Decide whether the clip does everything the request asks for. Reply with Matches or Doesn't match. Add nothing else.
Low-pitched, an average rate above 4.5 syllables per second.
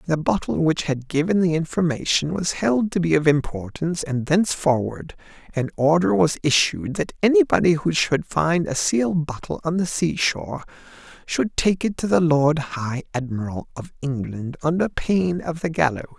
Doesn't match